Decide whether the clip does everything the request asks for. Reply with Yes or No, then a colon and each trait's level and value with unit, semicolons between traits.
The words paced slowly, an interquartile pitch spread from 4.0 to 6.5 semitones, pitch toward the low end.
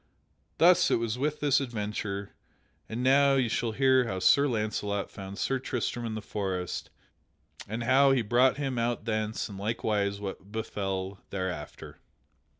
No: average, 150 wpm; average, 4.4 semitones; low, 110 Hz